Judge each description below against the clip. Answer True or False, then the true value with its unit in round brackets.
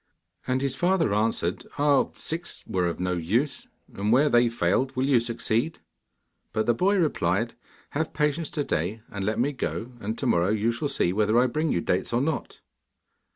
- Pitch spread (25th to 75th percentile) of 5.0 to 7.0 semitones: True (5.5 semitones)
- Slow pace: False (190 wpm)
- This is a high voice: False (120 Hz)